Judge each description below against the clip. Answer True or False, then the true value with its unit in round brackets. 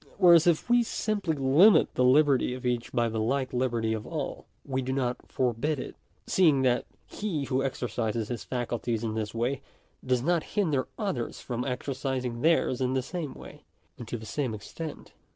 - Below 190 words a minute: True (180 wpm)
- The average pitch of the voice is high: False (130 Hz)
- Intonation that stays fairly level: False (4.0 semitones)